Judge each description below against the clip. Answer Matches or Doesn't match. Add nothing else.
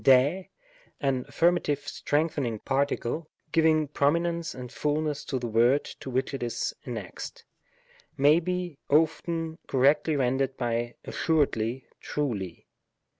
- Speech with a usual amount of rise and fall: Matches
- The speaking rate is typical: Doesn't match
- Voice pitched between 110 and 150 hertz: Matches